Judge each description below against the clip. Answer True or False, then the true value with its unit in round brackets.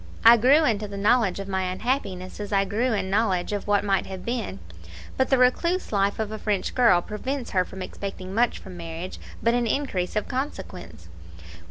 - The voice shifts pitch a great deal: False (4.2 semitones)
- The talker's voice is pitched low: False (205 Hz)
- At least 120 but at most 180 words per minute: False (195 wpm)